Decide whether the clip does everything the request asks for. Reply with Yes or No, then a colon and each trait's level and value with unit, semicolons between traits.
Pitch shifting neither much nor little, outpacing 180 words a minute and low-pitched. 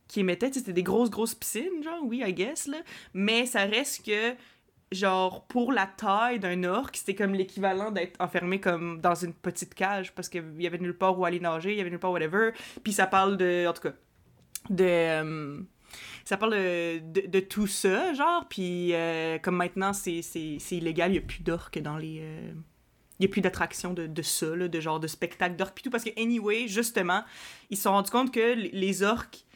No: average, 3.4 semitones; fast, 220 wpm; high, 190 Hz